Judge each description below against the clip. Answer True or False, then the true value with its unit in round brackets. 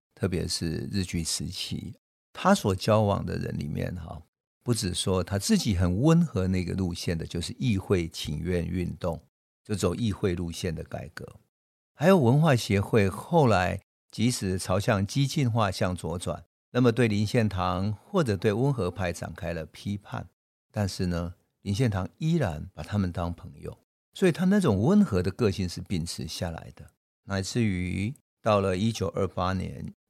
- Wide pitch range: False (4.4 semitones)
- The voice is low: True (100 Hz)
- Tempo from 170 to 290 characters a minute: True (245 characters per minute)